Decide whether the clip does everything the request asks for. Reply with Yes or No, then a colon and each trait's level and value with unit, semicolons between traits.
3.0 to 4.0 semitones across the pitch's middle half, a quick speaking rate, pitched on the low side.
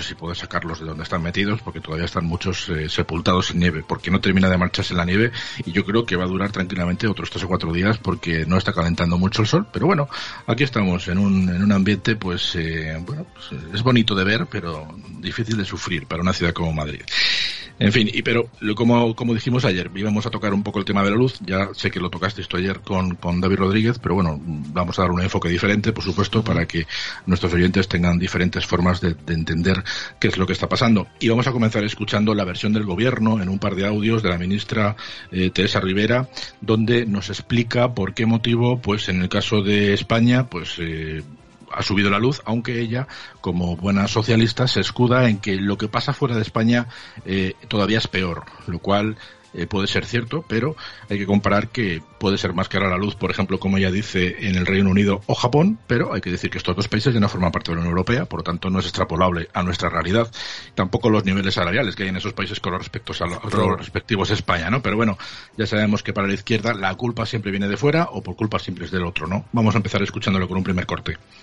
Yes: average, 3.6 semitones; fast, 235 wpm; low, 100 Hz